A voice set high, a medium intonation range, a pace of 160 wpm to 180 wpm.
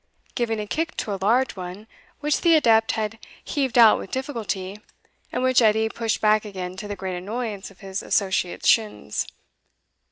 Yes: high, 215 Hz; average, 3.5 semitones; average, 170 wpm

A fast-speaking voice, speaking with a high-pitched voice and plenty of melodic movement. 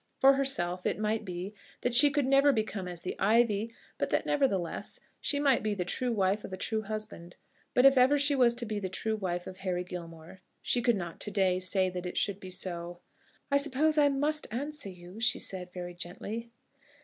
Yes: fast, 210 wpm; high, 210 Hz; wide, 5.9 semitones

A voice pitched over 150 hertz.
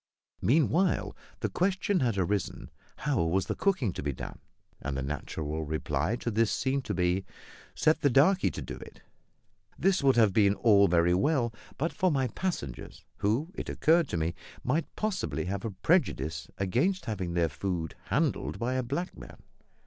No: low, 110 Hz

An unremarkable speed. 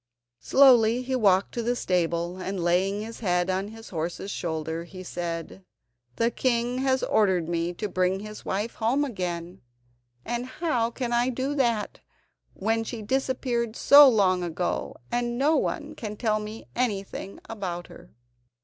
Yes: average, 155 wpm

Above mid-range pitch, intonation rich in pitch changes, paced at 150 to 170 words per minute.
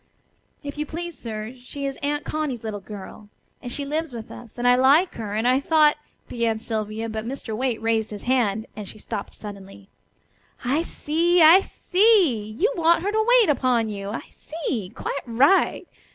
No: very high, 250 Hz; wide, 5.9 semitones; average, 185 wpm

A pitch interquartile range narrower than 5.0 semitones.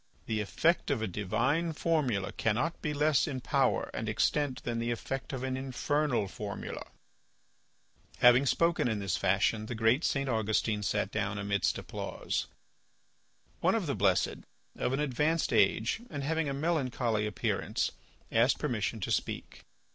No: wide, 5.6 semitones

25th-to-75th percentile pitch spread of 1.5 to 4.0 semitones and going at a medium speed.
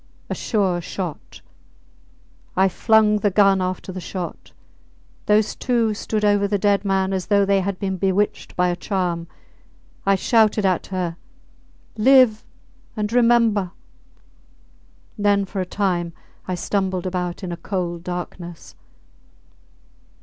No: narrow, 2.4 semitones; slow, 130 wpm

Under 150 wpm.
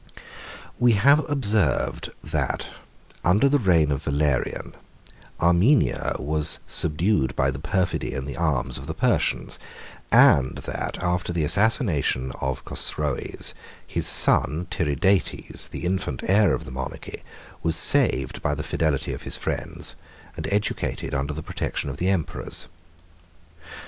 Yes: slow, 135 wpm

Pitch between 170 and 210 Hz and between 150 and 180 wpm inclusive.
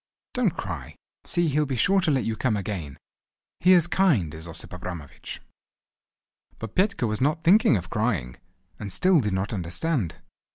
No: low, 115 Hz; average, 165 wpm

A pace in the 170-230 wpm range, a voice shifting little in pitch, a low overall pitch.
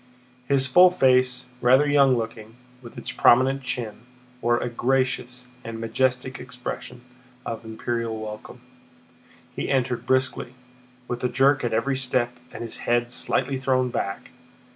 No: average, 140 wpm; narrow, 1.8 semitones; low, 125 Hz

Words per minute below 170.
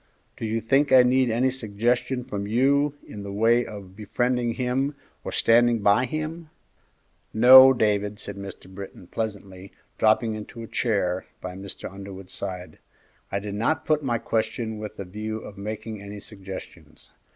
Yes: average, 160 wpm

